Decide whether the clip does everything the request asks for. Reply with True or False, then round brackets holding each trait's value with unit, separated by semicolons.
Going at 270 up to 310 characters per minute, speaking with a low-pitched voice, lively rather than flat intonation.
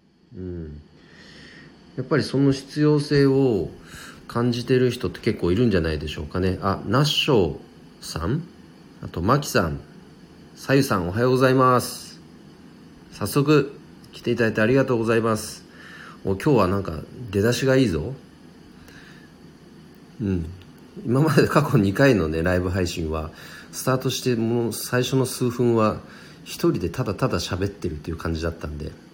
True (300 characters per minute; 115 Hz; 6.4 semitones)